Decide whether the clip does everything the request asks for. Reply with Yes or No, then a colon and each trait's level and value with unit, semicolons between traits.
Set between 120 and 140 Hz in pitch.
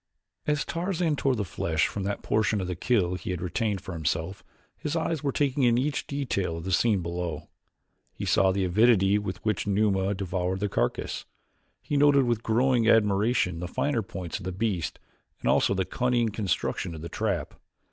No: low, 100 Hz